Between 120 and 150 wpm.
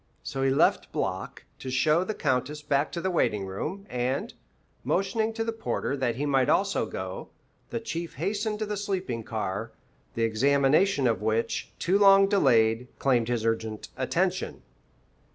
No: average, 160 wpm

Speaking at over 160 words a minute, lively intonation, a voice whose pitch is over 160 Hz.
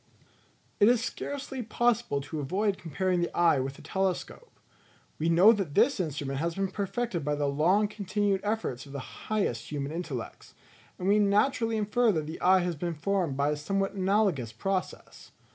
Yes: average, 175 wpm; wide, 5.7 semitones; medium, 185 Hz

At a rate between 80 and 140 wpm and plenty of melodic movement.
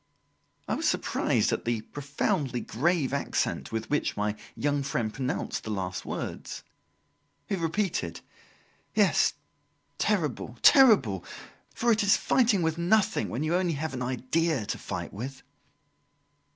Yes: slow, 135 wpm; wide, 6.6 semitones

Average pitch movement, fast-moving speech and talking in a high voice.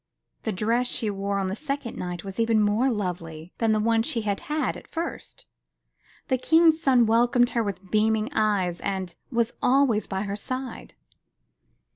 No: average, 3.7 semitones; average, 170 wpm; high, 220 Hz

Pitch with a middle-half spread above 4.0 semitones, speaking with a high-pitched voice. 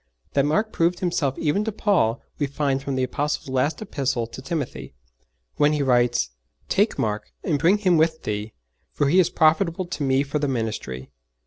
No: average, 4.4 semitones; medium, 145 Hz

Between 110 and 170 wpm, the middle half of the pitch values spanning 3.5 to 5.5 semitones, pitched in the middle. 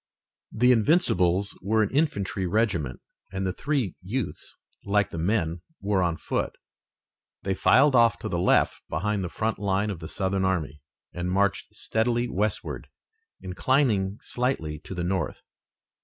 No: average, 145 wpm; average, 3.9 semitones; low, 100 Hz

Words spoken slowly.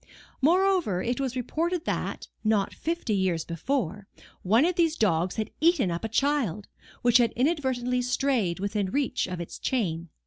No: average, 160 wpm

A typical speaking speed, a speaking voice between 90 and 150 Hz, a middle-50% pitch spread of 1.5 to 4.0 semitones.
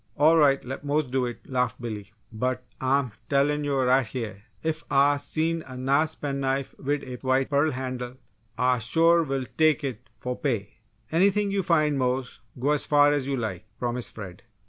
Yes: average, 185 wpm; low, 135 Hz; average, 2.8 semitones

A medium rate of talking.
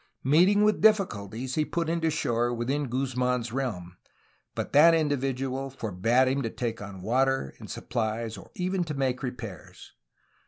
Yes: average, 160 wpm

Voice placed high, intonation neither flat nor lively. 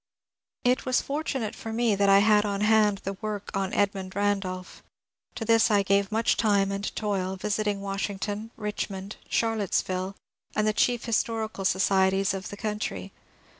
No: high, 205 Hz; narrow, 1.8 semitones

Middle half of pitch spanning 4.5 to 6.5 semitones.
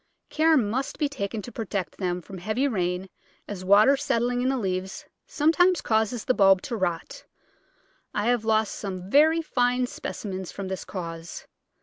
Yes: average, 5.2 semitones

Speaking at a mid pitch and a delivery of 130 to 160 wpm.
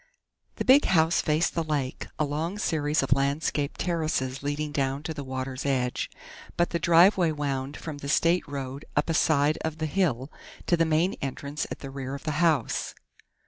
No: medium, 150 Hz; average, 185 wpm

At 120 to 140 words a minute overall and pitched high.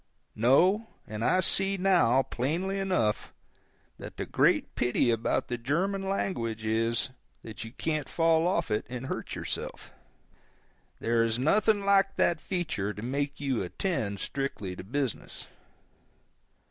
No: slow, 135 wpm; low, 135 Hz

